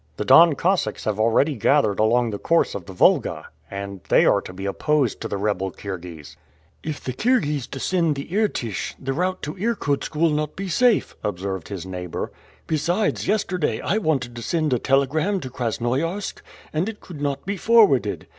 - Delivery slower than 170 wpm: No, average, 180 wpm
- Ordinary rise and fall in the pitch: No, wide, 8.3 semitones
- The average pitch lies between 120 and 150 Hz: Yes, medium, 140 Hz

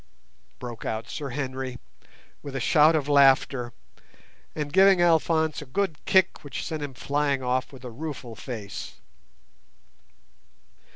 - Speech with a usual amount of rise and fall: Yes, average, 3.5 semitones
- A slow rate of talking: Yes, slow, 130 wpm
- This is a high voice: No, medium, 140 Hz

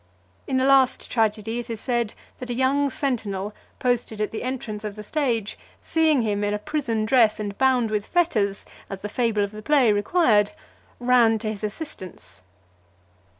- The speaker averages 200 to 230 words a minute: No, average, 175 wpm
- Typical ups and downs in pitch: Yes, average, 3.8 semitones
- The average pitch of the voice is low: No, high, 225 Hz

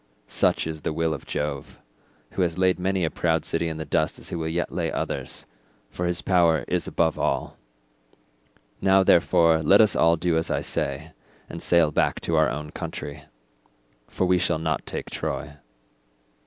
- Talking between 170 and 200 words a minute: Yes, average, 180 wpm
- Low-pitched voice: Yes, very low, 80 Hz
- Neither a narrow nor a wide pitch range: No, narrow, 2.0 semitones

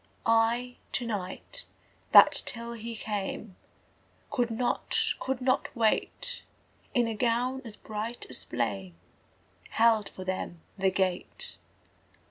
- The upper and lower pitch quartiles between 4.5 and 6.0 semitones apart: No, average, 4.0 semitones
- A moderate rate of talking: No, slow, 115 wpm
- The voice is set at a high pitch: Yes, high, 225 Hz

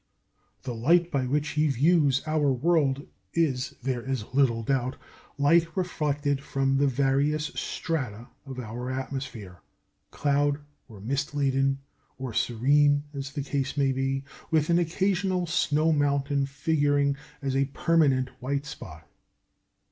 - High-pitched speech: No, medium, 140 Hz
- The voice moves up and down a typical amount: No, narrow, 2.1 semitones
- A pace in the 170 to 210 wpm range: No, slow, 135 wpm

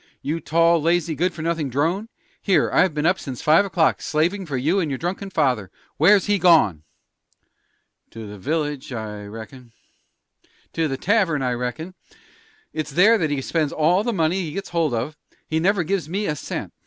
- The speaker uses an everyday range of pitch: Yes, average, 4.7 semitones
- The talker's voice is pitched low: No, medium, 160 Hz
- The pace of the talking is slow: No, average, 185 wpm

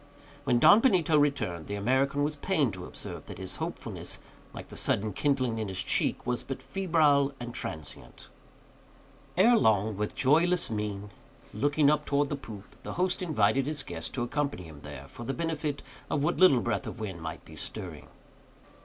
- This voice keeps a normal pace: Yes, average, 180 wpm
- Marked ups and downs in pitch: Yes, wide, 6.4 semitones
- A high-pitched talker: No, low, 135 Hz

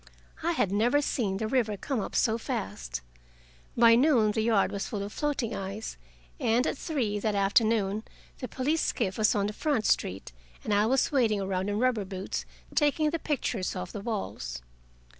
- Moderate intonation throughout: Yes, average, 4.2 semitones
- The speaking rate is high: No, average, 180 wpm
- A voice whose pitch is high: Yes, high, 220 Hz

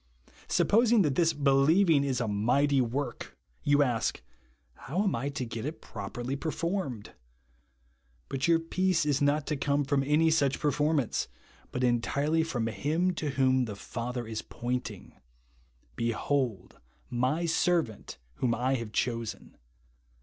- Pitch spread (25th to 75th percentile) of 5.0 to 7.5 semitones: No, average, 4.6 semitones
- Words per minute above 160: No, average, 145 wpm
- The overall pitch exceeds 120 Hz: Yes, low, 135 Hz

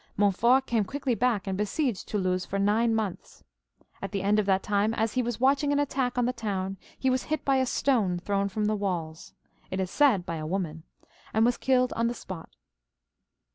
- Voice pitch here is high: Yes, high, 215 Hz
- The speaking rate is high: Yes, fast, 215 wpm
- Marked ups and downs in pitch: No, average, 4.5 semitones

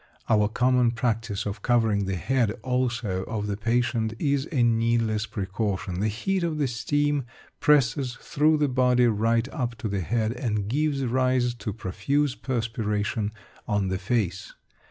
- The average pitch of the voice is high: No, low, 115 Hz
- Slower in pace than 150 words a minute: No, average, 155 wpm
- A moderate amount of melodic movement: Yes, average, 3.4 semitones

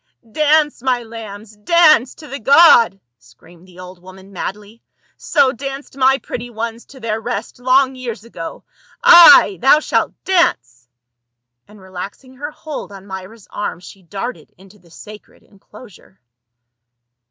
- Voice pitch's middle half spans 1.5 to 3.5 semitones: No, wide, 5.6 semitones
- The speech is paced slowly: No, average, 155 wpm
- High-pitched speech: Yes, high, 220 Hz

